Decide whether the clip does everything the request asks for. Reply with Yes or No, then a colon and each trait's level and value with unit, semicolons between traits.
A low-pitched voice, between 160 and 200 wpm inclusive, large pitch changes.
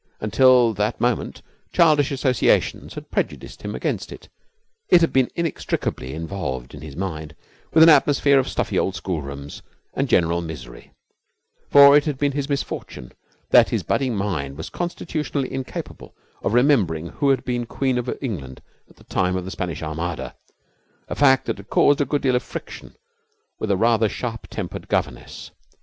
Yes: low, 115 Hz; average, 165 wpm; wide, 8.6 semitones